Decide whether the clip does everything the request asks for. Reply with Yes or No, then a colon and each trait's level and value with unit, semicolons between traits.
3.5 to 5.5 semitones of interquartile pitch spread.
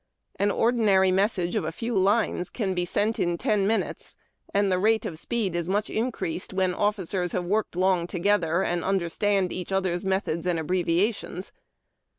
No: narrow, 2.6 semitones